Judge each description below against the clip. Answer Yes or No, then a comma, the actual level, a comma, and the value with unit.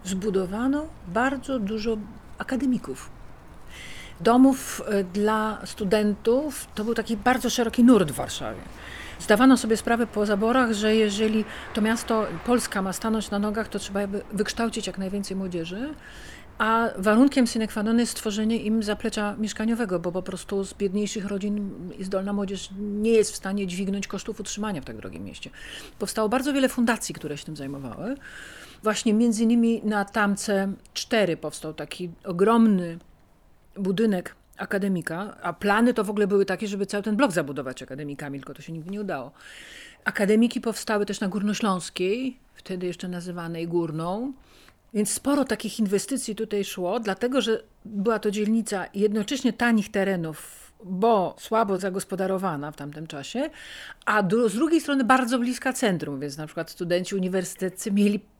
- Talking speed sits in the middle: Yes, average, 150 wpm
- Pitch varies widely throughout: No, average, 3.1 semitones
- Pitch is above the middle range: Yes, high, 210 Hz